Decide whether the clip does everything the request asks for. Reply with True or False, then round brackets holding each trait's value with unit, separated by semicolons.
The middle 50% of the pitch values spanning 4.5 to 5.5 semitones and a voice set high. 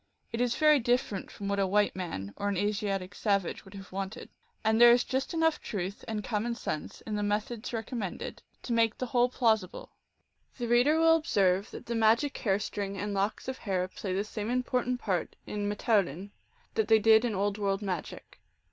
False (3.3 semitones; 210 Hz)